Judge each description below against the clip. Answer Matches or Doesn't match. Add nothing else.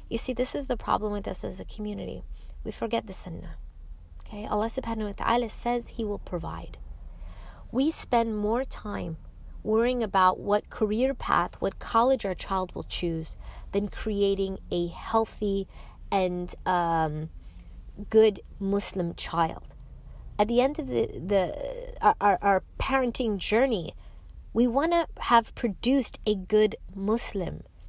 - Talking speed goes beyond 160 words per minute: Doesn't match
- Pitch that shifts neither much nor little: Matches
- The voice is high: Matches